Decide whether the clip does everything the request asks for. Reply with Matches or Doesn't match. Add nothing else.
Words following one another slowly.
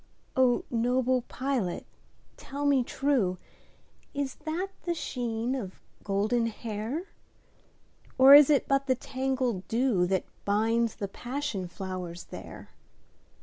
Matches